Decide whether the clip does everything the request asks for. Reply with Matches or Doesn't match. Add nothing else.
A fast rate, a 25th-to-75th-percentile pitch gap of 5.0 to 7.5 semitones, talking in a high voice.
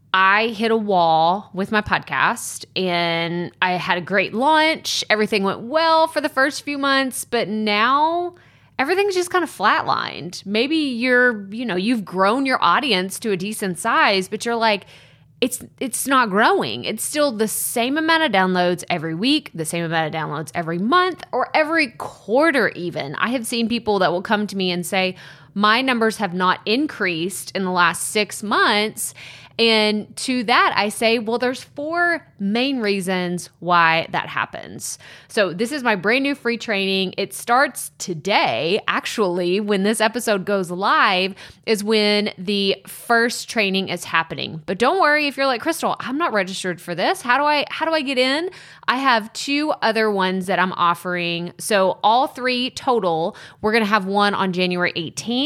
Doesn't match